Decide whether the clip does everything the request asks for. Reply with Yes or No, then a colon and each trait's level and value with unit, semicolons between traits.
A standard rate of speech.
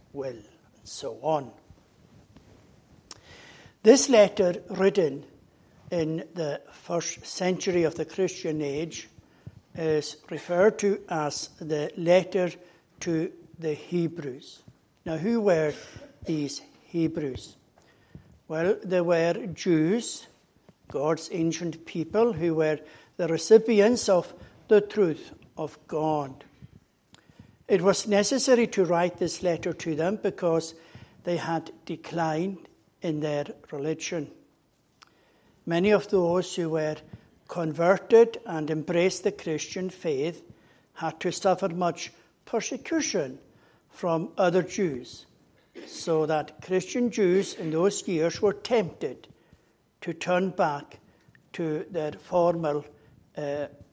No: slow, 105 wpm